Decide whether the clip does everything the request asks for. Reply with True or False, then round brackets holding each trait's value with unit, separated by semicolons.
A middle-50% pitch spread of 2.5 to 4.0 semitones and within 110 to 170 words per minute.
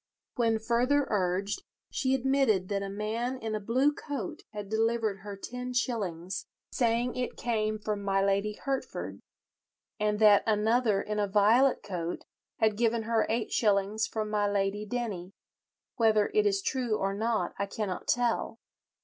True (3.0 semitones; 150 wpm)